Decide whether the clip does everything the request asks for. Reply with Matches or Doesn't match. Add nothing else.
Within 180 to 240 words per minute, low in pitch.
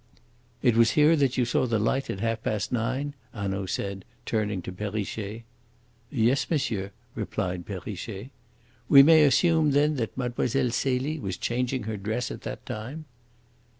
Doesn't match